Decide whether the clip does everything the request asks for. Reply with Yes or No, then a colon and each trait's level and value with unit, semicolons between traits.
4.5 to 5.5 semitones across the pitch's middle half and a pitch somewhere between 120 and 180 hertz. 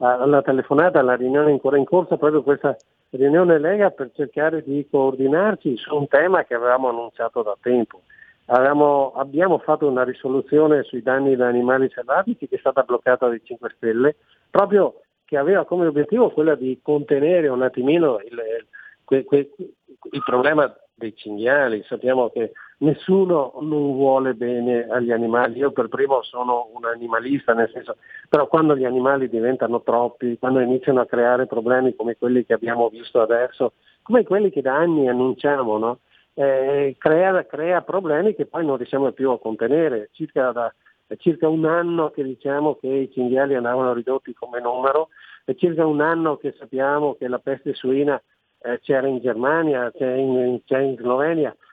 No: average, 3.4 semitones; low, 135 Hz